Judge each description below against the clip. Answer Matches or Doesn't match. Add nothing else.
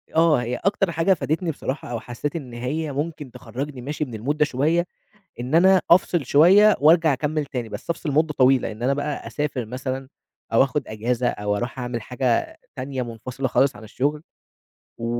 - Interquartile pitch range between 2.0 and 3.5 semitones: Doesn't match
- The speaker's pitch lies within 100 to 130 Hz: Doesn't match